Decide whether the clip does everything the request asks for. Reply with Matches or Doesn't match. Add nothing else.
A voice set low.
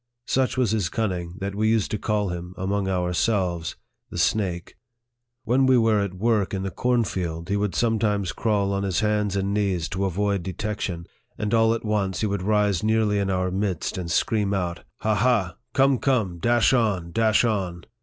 Matches